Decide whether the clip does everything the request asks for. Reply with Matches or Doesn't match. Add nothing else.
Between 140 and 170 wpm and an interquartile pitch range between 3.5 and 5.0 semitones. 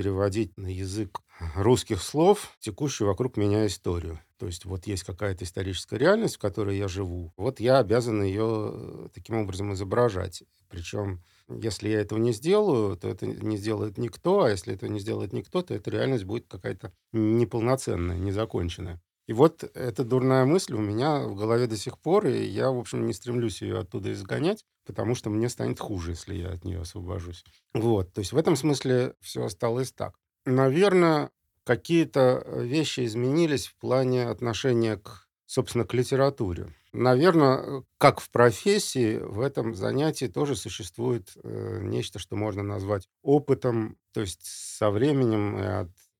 Matches